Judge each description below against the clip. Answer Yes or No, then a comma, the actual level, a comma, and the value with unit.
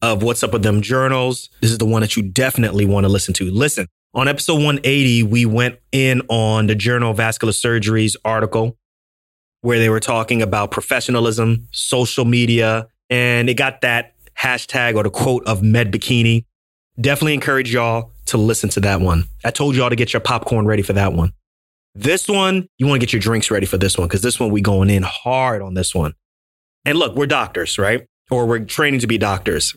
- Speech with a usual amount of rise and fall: Yes, average, 3.1 semitones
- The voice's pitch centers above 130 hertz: No, low, 115 Hz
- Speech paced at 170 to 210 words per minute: Yes, fast, 205 wpm